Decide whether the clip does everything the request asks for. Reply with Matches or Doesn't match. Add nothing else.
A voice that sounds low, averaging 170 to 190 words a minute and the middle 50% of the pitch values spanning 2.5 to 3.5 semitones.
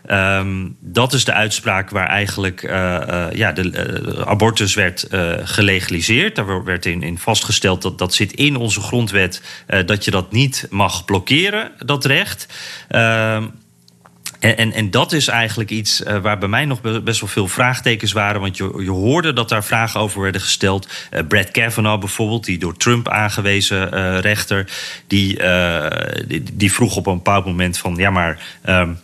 Matches